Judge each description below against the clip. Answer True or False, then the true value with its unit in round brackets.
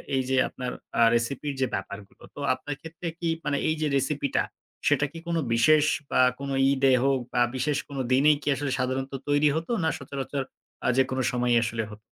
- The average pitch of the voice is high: False (135 Hz)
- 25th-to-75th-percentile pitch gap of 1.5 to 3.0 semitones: True (2.5 semitones)